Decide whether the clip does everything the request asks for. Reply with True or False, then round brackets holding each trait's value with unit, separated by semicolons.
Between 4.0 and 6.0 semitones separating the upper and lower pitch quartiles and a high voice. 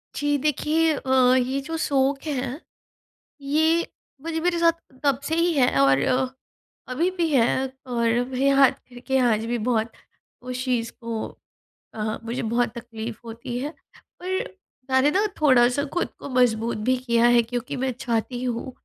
False (3.5 semitones; 255 Hz)